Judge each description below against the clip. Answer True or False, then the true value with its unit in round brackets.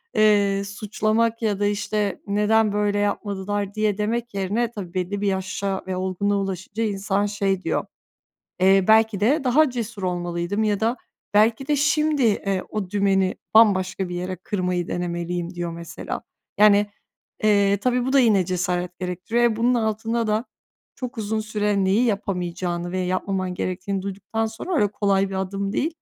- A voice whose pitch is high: True (200 Hz)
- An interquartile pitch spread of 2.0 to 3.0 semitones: True (2.7 semitones)